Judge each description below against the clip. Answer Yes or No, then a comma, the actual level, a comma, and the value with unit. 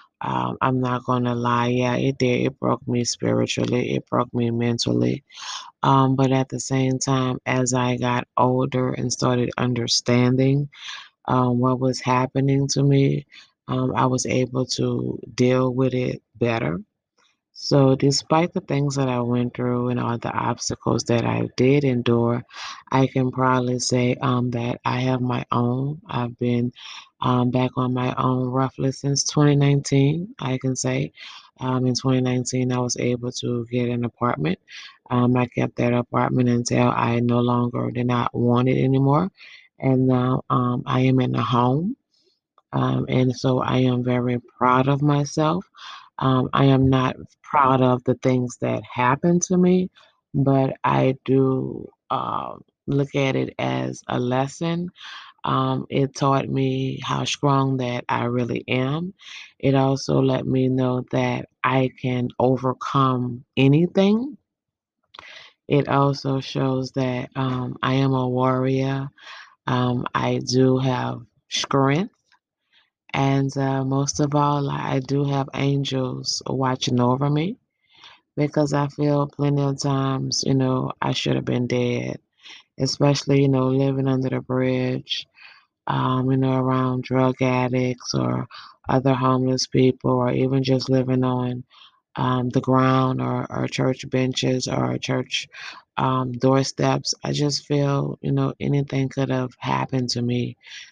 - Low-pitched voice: Yes, low, 130 Hz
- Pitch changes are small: Yes, narrow, 1.6 semitones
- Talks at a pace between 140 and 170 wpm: Yes, average, 150 wpm